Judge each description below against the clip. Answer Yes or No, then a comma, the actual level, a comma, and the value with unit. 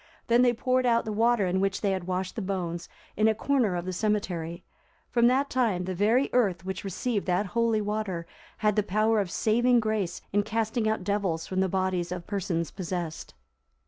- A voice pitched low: No, high, 205 Hz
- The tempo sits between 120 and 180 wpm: No, average, 200 wpm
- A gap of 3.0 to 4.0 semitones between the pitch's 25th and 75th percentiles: Yes, average, 3.5 semitones